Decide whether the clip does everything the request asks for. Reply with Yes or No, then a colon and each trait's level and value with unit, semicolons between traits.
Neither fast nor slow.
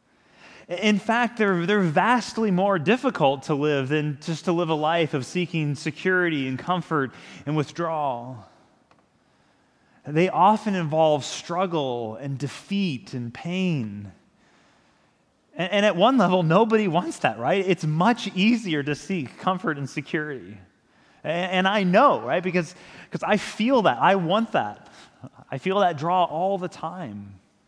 Yes: average, 145 wpm